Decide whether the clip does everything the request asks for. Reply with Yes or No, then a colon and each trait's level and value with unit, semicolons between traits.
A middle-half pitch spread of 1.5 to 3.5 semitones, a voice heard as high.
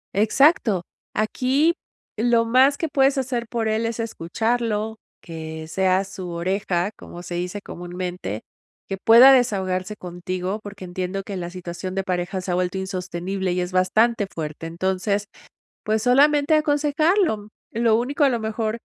No: average, 4.5 semitones; high, 200 Hz